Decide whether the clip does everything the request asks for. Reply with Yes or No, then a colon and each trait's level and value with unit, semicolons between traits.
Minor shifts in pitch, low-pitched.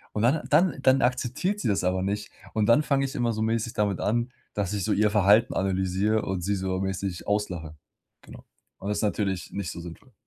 No: average, 3.5 semitones; low, 105 Hz